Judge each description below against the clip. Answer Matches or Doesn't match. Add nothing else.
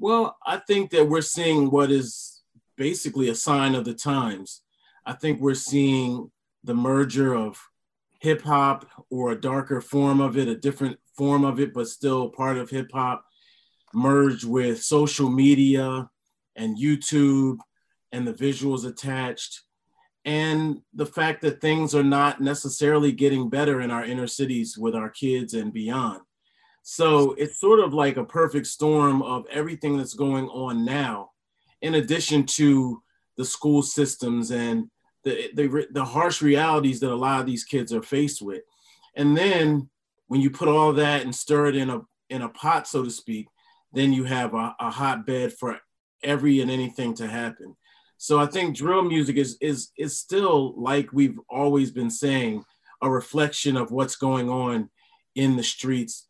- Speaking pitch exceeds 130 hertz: Matches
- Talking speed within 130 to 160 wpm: Doesn't match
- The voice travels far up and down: Doesn't match